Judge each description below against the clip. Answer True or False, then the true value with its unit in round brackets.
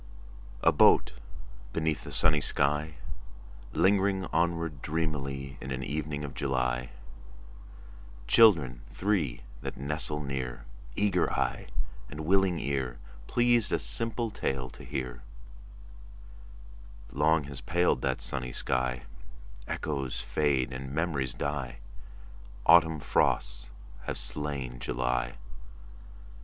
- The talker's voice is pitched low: True (70 Hz)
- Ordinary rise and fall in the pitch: True (4.2 semitones)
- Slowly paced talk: True (105 wpm)